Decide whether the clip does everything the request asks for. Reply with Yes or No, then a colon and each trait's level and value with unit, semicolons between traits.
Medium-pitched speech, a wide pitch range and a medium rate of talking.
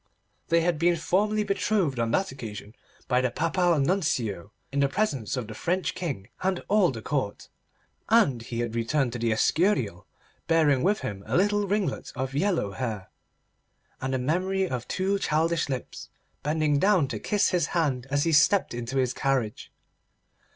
Yes: medium, 145 Hz; wide, 7.1 semitones; average, 170 wpm